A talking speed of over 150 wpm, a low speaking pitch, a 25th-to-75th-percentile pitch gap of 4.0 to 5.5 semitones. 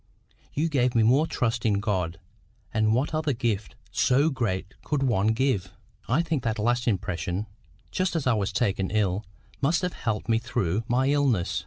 Yes: average, 175 wpm; low, 115 Hz; average, 5.0 semitones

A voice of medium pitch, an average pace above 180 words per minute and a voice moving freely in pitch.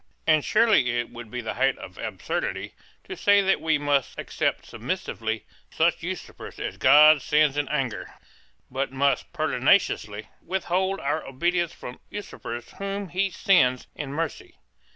No: medium, 145 Hz; average, 145 wpm; wide, 6.2 semitones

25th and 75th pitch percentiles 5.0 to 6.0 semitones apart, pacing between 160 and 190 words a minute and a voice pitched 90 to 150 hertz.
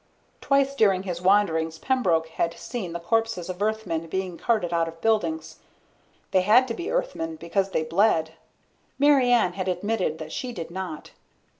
No: average, 5.3 semitones; average, 165 wpm; high, 190 Hz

